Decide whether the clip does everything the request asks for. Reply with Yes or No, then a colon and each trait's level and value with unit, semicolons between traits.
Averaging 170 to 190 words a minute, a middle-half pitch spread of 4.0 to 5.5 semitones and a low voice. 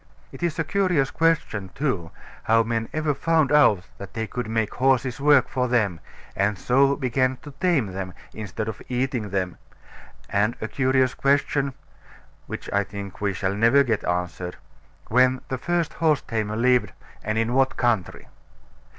No: average, 160 wpm; average, 5.0 semitones; low, 120 Hz